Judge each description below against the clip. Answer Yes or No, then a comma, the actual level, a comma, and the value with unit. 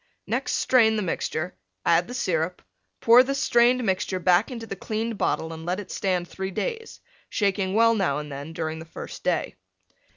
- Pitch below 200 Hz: Yes, high, 190 Hz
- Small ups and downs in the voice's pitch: No, average, 5.3 semitones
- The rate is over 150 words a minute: Yes, average, 185 wpm